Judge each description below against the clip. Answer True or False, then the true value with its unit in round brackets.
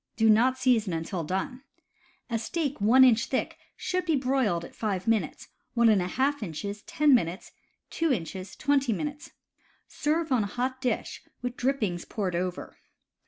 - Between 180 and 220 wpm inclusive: False (140 wpm)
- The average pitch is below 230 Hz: False (235 Hz)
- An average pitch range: False (5.7 semitones)